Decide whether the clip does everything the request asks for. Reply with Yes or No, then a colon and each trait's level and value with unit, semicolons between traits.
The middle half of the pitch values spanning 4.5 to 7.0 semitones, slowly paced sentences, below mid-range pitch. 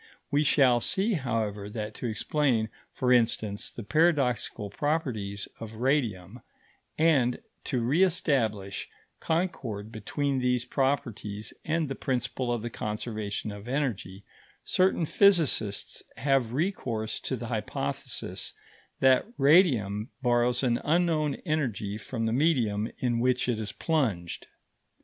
Yes: average, 5.2 semitones; slow, 120 wpm; low, 125 Hz